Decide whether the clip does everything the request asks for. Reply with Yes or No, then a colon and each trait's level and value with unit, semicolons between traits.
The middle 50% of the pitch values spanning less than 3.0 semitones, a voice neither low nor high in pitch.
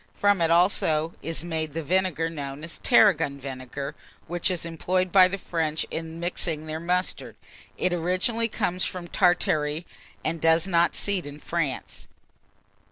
Yes: narrow, 2.6 semitones; medium, 170 Hz